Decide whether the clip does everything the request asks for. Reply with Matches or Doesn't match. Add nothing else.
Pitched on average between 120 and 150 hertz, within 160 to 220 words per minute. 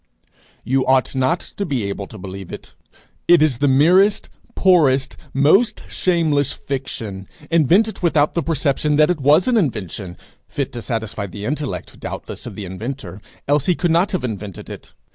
Matches